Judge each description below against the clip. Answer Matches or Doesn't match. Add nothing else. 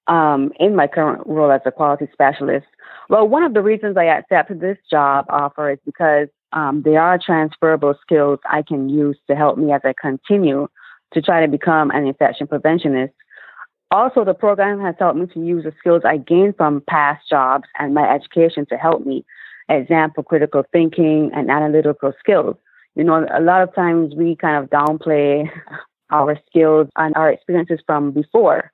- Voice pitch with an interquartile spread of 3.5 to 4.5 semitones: Doesn't match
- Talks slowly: Doesn't match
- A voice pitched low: Doesn't match